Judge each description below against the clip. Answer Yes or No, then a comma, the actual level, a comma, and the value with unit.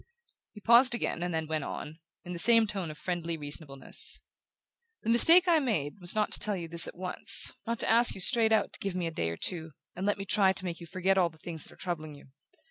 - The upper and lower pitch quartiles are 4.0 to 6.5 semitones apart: Yes, average, 4.7 semitones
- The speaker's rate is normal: No, fast, 255 wpm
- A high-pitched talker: No, medium, 180 Hz